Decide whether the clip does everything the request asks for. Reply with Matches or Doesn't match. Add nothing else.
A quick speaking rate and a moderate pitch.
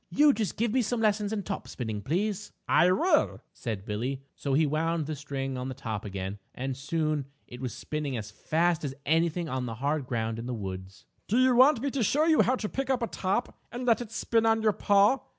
Matches